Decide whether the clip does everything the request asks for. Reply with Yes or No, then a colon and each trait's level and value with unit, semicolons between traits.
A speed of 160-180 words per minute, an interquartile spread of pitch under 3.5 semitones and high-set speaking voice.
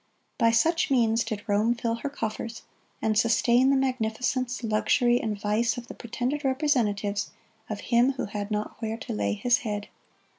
Yes: average, 170 wpm; average, 2.9 semitones; high, 230 Hz